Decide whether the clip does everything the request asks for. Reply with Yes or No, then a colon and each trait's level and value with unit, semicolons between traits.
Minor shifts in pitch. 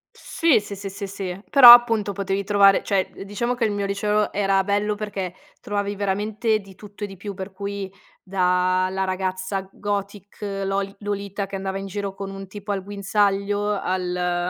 Yes: narrow, 1.2 semitones